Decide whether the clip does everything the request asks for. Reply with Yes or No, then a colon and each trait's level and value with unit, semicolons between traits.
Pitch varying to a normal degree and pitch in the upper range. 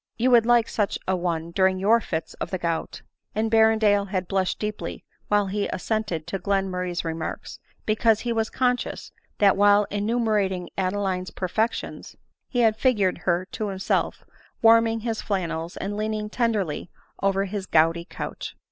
Yes: average, 3.1 semitones; high, 200 Hz